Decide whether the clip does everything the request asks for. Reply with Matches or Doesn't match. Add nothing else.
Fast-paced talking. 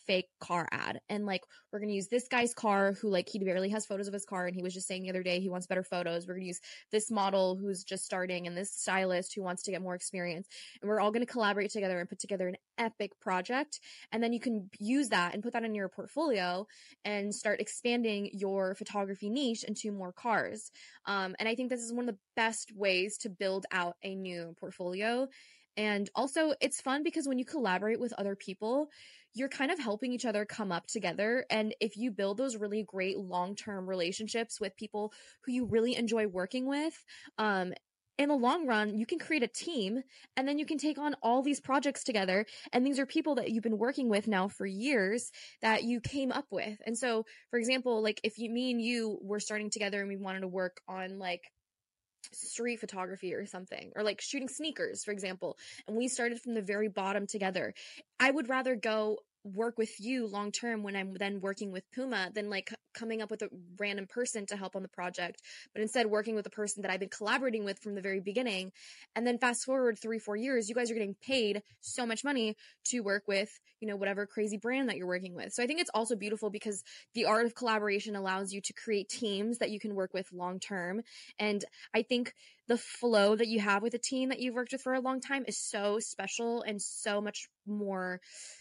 Matches